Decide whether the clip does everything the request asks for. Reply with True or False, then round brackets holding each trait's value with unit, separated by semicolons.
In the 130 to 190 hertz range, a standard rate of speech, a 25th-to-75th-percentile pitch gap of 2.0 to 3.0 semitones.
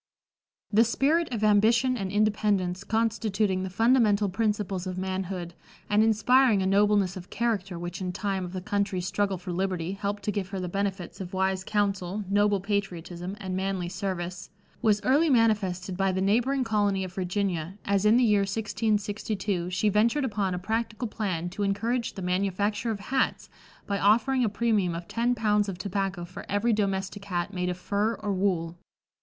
False (200 Hz; 180 wpm; 2.4 semitones)